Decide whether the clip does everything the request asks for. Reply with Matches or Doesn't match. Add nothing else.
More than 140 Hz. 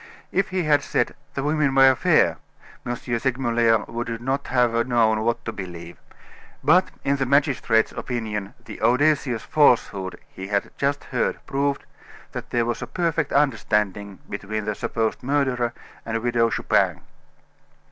Doesn't match